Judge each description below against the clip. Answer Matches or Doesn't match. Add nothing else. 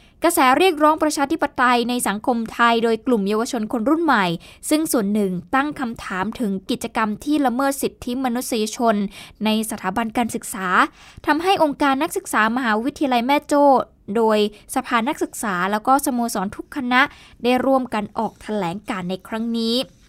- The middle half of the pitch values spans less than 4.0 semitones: Doesn't match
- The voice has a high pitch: Matches